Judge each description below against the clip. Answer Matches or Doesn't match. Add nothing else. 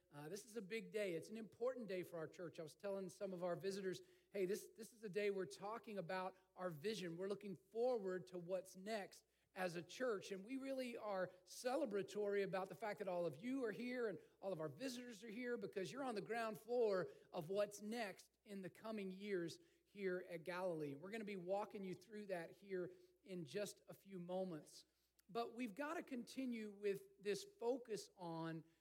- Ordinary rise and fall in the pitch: Matches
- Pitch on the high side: Matches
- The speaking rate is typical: Doesn't match